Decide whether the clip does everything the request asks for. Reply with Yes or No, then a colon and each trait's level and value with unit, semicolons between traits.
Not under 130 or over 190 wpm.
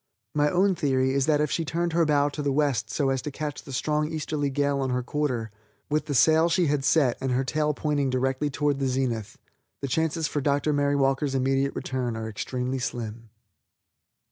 No: fast, 205 wpm